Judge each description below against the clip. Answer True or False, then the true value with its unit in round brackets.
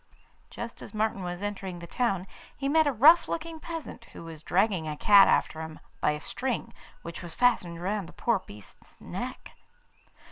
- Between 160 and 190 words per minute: True (180 wpm)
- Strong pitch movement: True (6.4 semitones)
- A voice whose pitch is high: True (195 Hz)